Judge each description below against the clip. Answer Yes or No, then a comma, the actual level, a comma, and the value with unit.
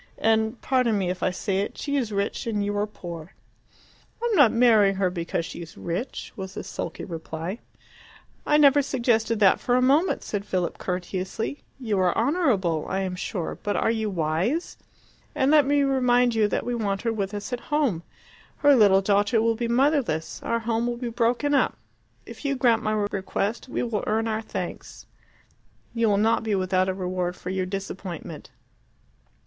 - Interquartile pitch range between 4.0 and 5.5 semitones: Yes, average, 4.3 semitones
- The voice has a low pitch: No, high, 215 Hz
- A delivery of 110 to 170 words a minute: No, average, 190 wpm